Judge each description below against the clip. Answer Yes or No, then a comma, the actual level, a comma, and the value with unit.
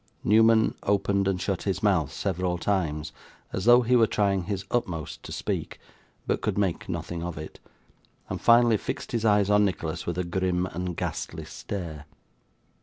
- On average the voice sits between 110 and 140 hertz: No, very low, 95 Hz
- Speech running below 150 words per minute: No, average, 170 wpm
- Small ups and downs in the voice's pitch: No, average, 3.1 semitones